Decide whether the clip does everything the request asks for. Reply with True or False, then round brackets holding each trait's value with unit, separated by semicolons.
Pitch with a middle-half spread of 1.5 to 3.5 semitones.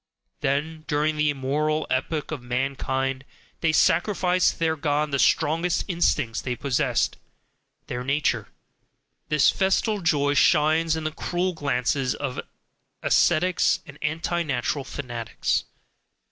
True (3.2 semitones)